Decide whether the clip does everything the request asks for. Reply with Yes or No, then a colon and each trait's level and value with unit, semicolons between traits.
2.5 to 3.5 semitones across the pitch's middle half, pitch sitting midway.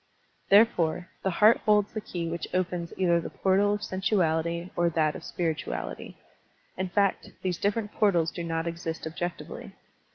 Yes: average, 3.0 semitones; medium, 175 Hz